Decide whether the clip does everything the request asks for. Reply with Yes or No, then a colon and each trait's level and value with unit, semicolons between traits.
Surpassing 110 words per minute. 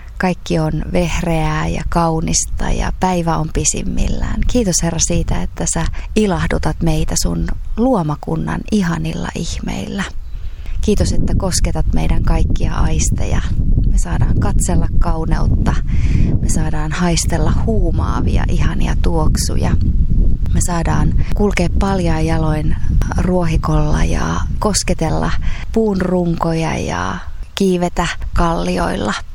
No: average, 100 wpm